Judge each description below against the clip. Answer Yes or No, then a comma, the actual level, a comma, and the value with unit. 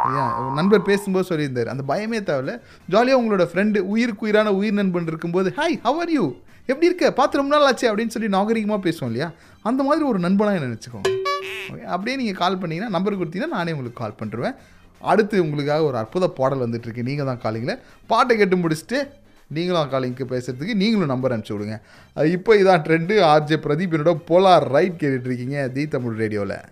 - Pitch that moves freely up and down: Yes, wide, 8.0 semitones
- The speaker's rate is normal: No, fast, 170 wpm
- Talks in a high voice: No, medium, 175 Hz